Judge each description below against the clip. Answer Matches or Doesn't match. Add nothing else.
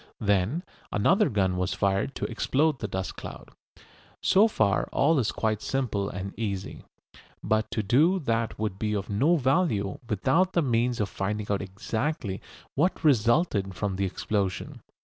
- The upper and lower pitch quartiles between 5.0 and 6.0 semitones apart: Matches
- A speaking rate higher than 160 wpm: Doesn't match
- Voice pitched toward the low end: Matches